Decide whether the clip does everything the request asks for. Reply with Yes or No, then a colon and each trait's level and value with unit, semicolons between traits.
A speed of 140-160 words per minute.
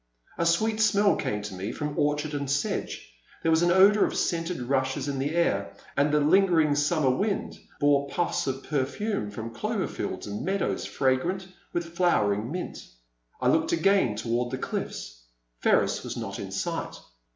No: average, 170 wpm